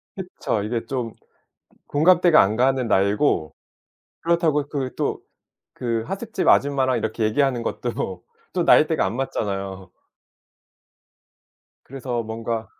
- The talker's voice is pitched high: No, low, 125 Hz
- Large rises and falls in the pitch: No, average, 4.6 semitones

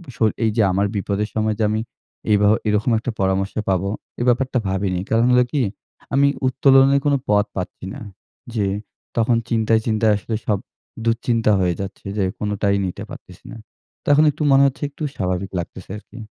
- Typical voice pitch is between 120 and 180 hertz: No, low, 110 Hz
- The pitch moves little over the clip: No, average, 3.8 semitones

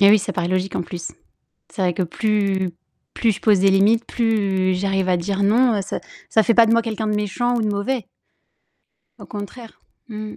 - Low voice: No, high, 205 Hz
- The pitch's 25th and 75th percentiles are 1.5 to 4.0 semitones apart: Yes, average, 2.8 semitones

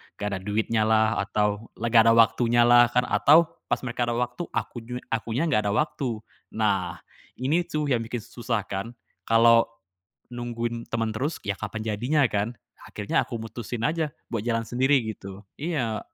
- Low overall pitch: Yes, low, 115 Hz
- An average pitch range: No, narrow, 2.1 semitones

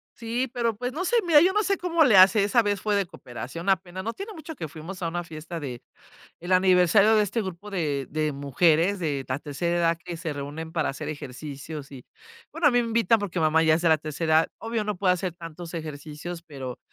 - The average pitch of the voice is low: No, medium, 175 Hz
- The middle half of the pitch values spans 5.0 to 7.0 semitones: Yes, average, 5.3 semitones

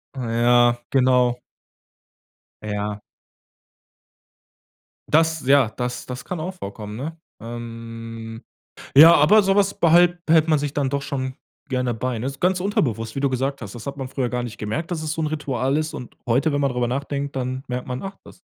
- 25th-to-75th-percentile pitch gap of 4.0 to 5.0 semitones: Yes, average, 4.3 semitones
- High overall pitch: No, low, 130 Hz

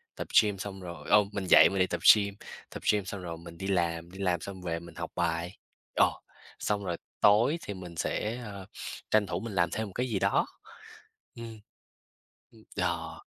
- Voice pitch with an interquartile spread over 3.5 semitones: No, average, 3.1 semitones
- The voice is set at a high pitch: No, very low, 95 Hz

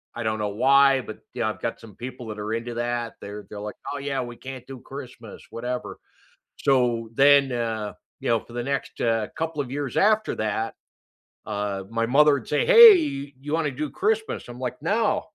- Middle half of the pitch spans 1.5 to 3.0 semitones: No, average, 3.7 semitones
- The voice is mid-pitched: No, low, 125 Hz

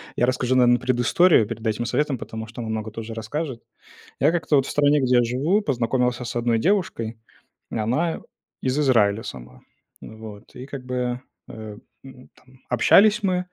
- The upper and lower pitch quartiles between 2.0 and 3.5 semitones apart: No, average, 4.1 semitones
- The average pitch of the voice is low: Yes, low, 125 Hz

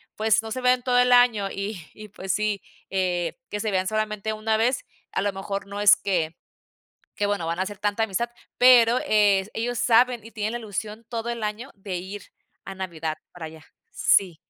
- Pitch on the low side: No, high, 210 Hz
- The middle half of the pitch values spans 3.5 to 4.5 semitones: No, average, 2.8 semitones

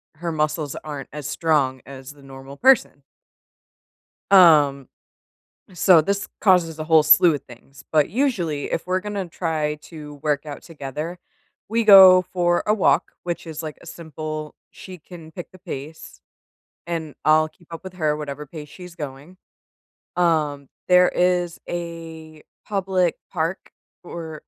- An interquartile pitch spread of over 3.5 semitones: No, average, 3.1 semitones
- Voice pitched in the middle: Yes, medium, 160 Hz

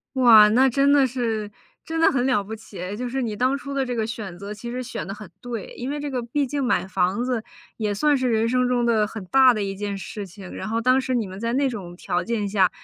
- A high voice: Yes, high, 230 Hz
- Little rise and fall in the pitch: No, average, 3.7 semitones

